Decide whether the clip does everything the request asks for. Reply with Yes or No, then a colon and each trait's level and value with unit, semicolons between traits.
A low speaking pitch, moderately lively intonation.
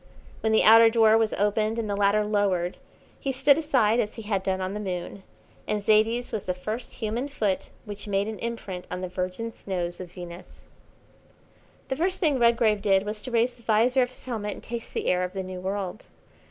No: high, 210 Hz; average, 3.3 semitones